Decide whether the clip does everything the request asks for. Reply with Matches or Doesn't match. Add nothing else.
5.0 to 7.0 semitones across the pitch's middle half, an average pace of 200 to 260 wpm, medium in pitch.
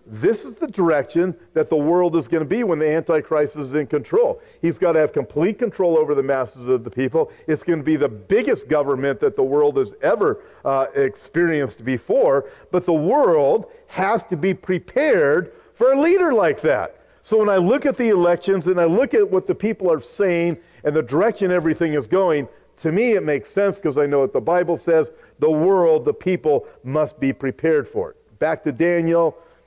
Matches